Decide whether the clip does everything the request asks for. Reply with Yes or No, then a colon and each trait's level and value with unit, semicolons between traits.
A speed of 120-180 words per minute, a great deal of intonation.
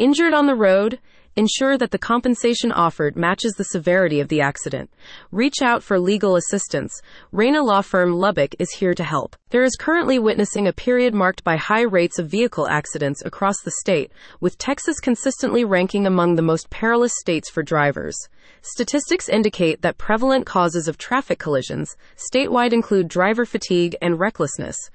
Yes: average, 165 wpm; wide, 5.7 semitones